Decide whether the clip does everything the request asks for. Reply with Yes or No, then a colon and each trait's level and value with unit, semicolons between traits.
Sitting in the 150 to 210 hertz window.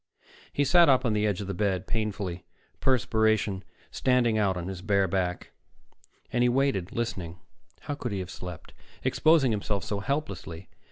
No: low, 105 Hz